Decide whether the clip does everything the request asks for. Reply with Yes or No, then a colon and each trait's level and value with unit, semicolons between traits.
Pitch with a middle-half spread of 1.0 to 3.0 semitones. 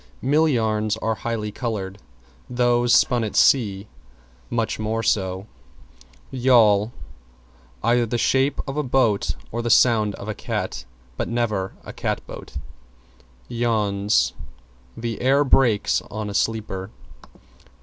Yes: average, 2.7 semitones